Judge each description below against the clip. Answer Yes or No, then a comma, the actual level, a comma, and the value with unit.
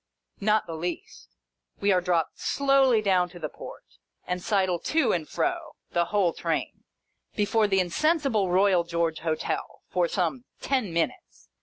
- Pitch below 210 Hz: Yes, high, 190 Hz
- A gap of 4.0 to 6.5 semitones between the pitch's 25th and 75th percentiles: Yes, average, 4.7 semitones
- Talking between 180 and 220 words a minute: No, average, 150 wpm